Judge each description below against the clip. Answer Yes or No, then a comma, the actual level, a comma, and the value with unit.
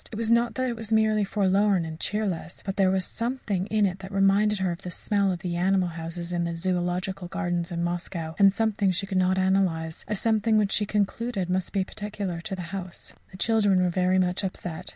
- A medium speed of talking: No, fast, 230 wpm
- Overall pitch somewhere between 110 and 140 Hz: No, high, 190 Hz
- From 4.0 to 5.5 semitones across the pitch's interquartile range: No, average, 2.7 semitones